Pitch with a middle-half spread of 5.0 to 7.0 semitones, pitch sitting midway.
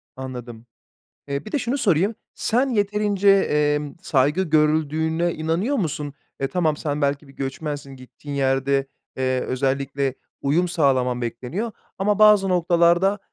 Yes: wide, 5.6 semitones; medium, 150 Hz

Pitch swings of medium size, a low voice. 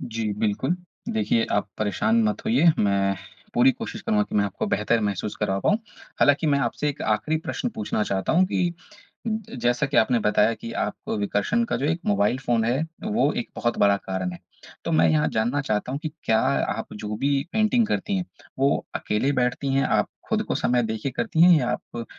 No: wide, 7.7 semitones; low, 125 Hz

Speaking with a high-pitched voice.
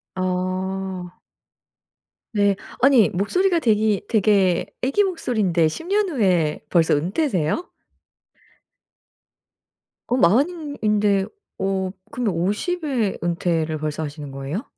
Yes: high, 195 Hz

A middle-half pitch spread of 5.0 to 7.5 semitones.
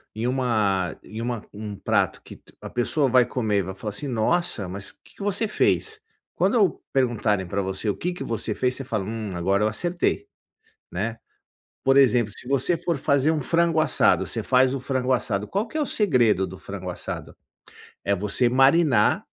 Yes: wide, 5.5 semitones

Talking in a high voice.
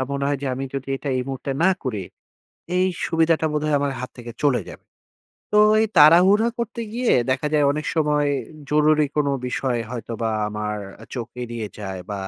No: medium, 140 Hz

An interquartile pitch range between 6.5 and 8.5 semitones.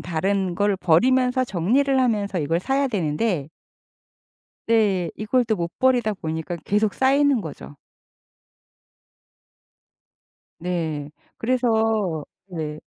Yes: wide, 6.8 semitones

